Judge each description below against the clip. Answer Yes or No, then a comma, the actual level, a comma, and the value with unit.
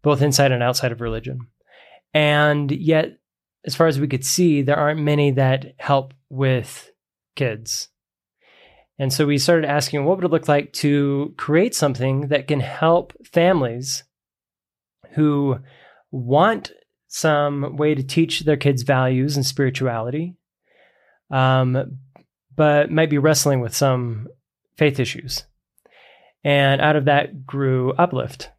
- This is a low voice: No, medium, 145 Hz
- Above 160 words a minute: No, slow, 135 wpm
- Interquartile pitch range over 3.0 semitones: No, narrow, 2.5 semitones